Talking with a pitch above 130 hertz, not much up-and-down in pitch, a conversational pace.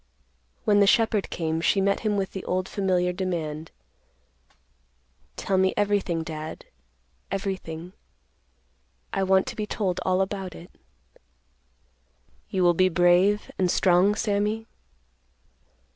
No: high, 190 Hz; narrow, 2.2 semitones; slow, 120 wpm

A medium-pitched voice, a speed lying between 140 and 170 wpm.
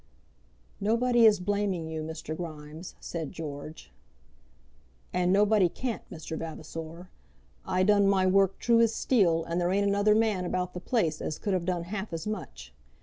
Yes: medium, 180 Hz; average, 160 wpm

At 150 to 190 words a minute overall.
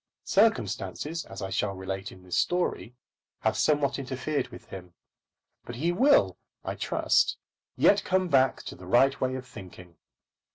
Yes: average, 155 wpm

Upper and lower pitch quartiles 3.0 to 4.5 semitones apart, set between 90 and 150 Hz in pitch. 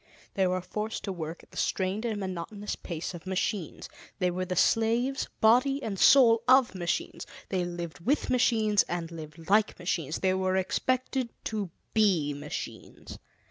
No: average, 4.2 semitones; high, 190 Hz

